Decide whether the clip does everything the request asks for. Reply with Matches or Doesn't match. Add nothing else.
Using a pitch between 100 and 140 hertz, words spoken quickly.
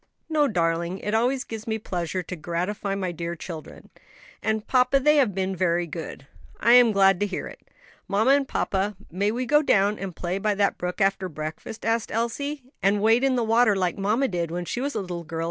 Doesn't match